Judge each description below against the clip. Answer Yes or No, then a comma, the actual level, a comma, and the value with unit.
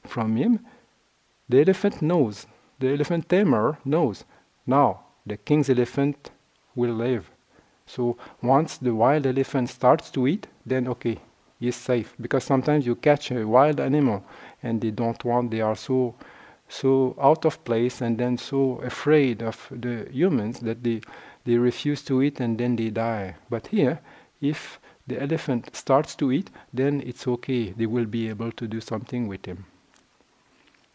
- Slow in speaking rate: No, average, 160 wpm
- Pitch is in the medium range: No, low, 125 Hz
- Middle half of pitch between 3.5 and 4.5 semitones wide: No, average, 3.0 semitones